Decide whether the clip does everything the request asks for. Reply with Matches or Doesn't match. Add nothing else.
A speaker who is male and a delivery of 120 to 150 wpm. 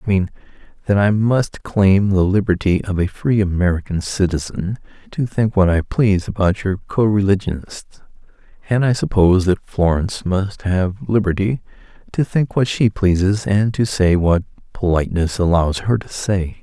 Doesn't match